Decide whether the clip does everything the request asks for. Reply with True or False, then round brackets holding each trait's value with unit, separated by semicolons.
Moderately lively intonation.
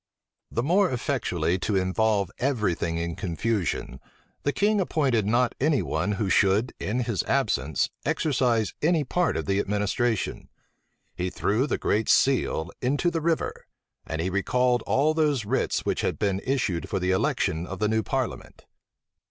False (6.0 semitones)